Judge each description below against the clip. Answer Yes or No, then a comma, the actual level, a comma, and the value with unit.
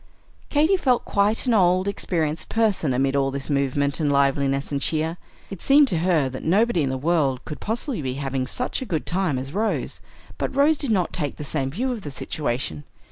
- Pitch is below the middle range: No, medium, 160 Hz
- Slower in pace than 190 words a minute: No, fast, 205 wpm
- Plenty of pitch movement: Yes, wide, 7.4 semitones